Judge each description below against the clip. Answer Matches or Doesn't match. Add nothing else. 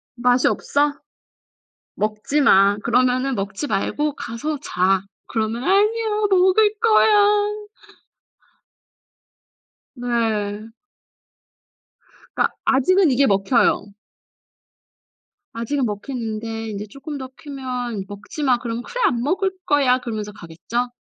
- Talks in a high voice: Matches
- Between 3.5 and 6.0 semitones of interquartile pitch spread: Matches